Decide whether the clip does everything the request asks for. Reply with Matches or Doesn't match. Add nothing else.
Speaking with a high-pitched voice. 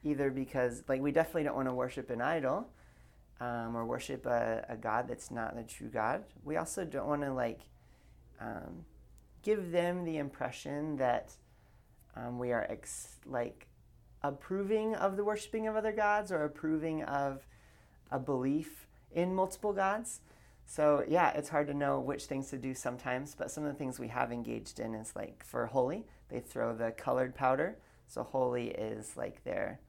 Doesn't match